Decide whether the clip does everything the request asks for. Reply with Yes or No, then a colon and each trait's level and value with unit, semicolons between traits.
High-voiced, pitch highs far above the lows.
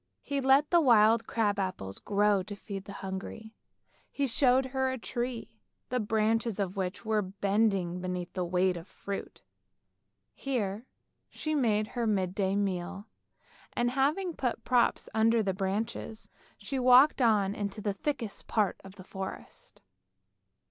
No: high, 215 Hz; average, 4.0 semitones